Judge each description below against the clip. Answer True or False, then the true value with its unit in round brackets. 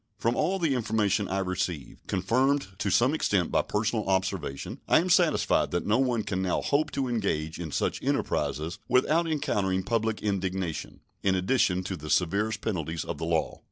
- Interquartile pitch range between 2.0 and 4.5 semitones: False (5.0 semitones)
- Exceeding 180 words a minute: False (175 wpm)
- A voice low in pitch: True (100 Hz)